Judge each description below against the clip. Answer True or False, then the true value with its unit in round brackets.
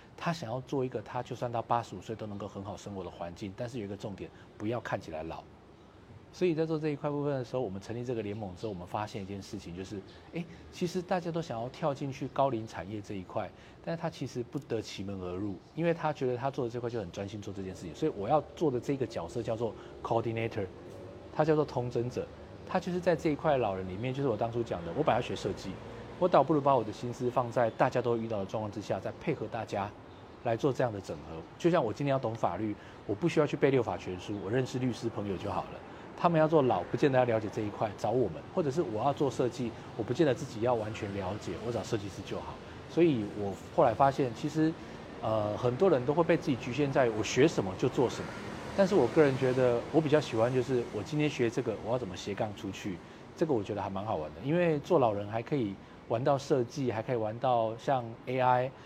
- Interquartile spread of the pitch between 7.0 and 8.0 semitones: False (5.3 semitones)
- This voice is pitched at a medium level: False (120 Hz)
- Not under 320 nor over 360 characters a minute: False (370 characters per minute)